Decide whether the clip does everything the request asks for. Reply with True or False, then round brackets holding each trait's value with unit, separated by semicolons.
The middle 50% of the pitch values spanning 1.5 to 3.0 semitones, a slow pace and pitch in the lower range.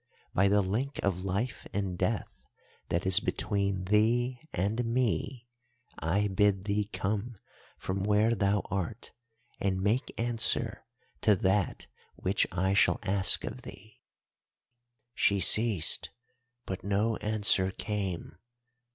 True (2.5 semitones; 120 wpm; 100 Hz)